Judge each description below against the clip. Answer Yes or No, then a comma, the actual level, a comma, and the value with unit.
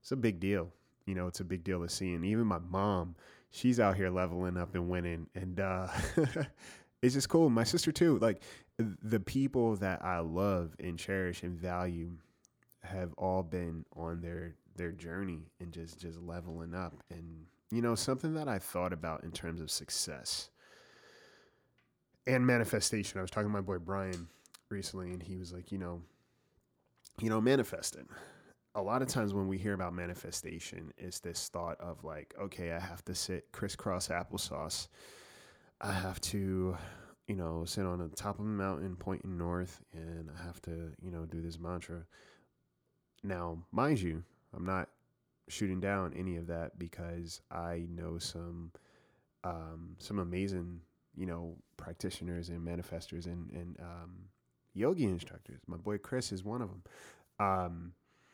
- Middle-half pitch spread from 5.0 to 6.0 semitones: No, average, 2.8 semitones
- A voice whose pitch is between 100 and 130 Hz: No, very low, 90 Hz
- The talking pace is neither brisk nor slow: Yes, average, 170 wpm